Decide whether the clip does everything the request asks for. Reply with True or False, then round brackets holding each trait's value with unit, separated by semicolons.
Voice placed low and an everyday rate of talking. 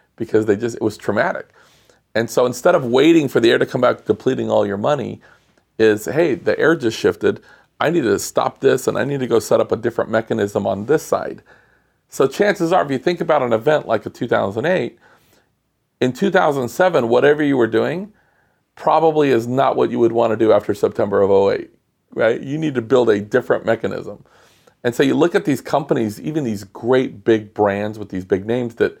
False (130 Hz; 210 wpm)